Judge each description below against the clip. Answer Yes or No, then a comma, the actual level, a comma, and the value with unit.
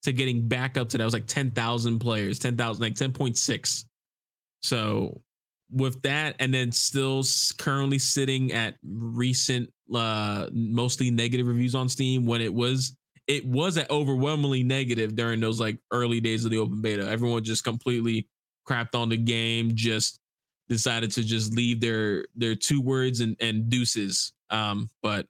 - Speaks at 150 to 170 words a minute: Yes, average, 160 wpm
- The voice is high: No, low, 120 Hz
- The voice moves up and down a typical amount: No, narrow, 2.3 semitones